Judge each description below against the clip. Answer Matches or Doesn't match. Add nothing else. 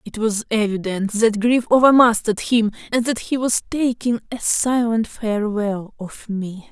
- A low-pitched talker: Doesn't match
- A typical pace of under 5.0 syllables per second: Matches